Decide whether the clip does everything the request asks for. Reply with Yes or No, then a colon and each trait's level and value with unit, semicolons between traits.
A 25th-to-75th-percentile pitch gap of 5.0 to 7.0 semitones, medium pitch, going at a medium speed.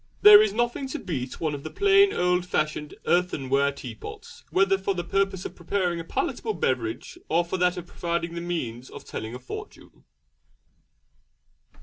Yes: wide, 5.6 semitones; medium, 175 Hz; average, 165 wpm